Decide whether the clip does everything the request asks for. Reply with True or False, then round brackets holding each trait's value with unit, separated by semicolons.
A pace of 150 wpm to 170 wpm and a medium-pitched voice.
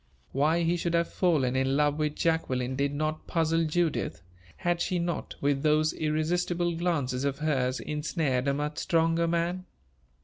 True (160 wpm; 155 Hz)